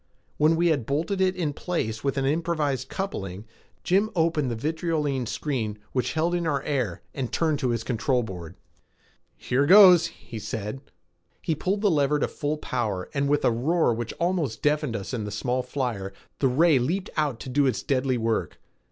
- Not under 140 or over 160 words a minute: No, average, 185 wpm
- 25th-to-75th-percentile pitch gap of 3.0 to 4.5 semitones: No, average, 5.3 semitones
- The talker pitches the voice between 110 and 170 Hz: Yes, medium, 140 Hz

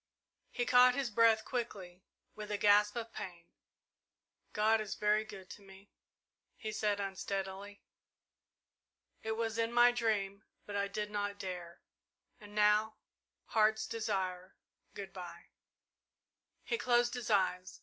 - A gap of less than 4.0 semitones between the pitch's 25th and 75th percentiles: Yes, narrow, 2.4 semitones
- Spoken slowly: Yes, slow, 130 wpm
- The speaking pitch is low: No, high, 210 Hz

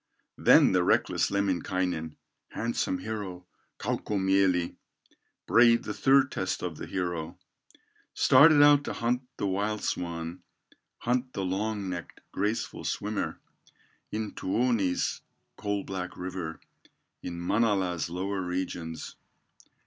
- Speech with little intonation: No, average, 3.5 semitones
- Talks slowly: Yes, slow, 110 wpm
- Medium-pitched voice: No, very low, 95 Hz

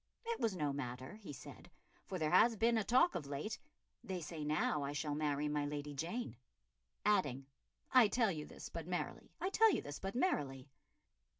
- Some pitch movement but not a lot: No, wide, 7.1 semitones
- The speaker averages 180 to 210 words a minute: Yes, average, 190 wpm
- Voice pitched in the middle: Yes, medium, 155 Hz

